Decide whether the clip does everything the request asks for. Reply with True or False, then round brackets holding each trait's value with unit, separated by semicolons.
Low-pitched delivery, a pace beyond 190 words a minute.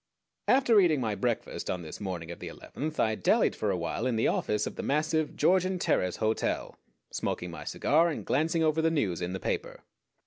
True (130 Hz; 200 wpm)